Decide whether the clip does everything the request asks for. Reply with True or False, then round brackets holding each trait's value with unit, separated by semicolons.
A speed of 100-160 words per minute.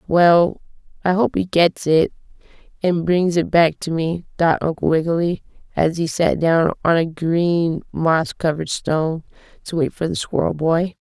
False (170 wpm)